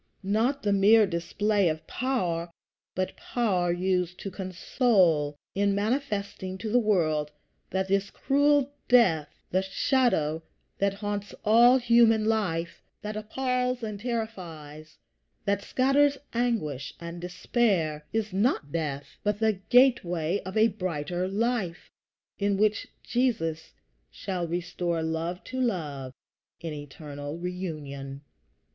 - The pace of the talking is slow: Yes, slow, 120 wpm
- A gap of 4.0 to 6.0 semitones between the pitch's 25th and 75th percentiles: Yes, average, 5.3 semitones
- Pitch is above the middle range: Yes, high, 195 Hz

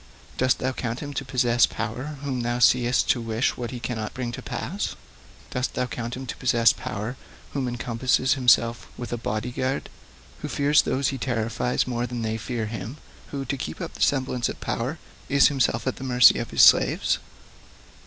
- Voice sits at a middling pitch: No, low, 125 Hz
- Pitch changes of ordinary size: No, narrow, 2.0 semitones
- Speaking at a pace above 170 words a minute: Yes, average, 195 wpm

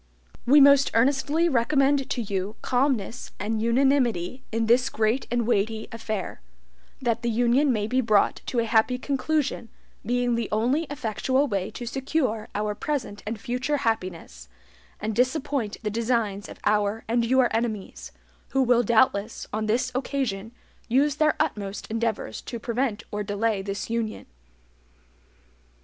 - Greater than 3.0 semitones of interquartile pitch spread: Yes, average, 3.5 semitones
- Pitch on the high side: Yes, high, 235 Hz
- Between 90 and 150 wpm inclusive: Yes, average, 145 wpm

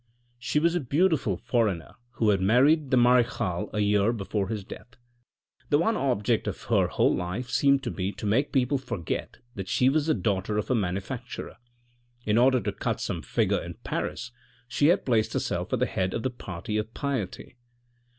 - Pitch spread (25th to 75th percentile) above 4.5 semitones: Yes, average, 5.0 semitones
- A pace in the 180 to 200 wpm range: Yes, average, 190 wpm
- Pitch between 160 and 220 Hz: No, low, 120 Hz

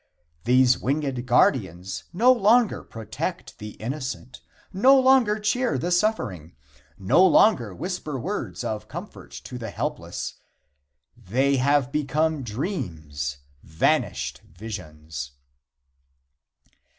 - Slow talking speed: Yes, slow, 100 wpm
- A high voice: No, low, 130 Hz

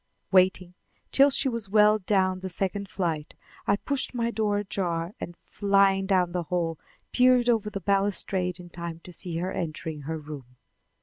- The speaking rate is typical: Yes, average, 170 wpm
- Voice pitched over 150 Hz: Yes, high, 190 Hz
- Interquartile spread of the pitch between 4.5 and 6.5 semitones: No, average, 3.2 semitones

